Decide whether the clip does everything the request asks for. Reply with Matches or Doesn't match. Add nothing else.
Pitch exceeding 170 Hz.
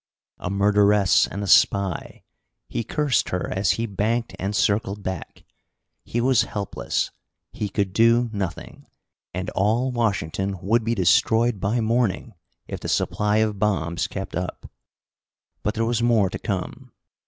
Doesn't match